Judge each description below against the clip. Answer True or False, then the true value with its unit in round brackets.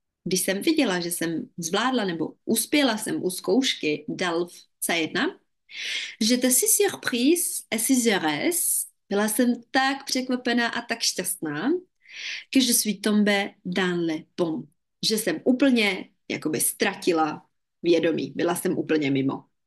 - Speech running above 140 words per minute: False (120 wpm)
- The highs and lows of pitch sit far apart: True (6.8 semitones)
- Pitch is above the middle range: True (215 Hz)